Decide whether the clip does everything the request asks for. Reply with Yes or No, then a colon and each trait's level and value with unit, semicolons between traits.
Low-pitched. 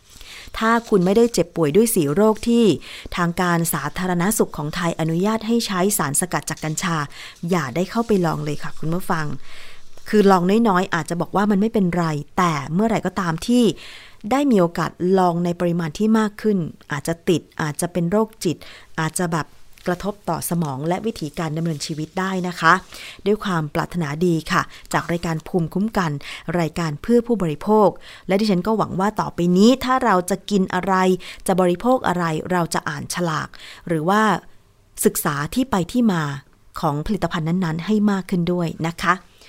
No: medium, 175 Hz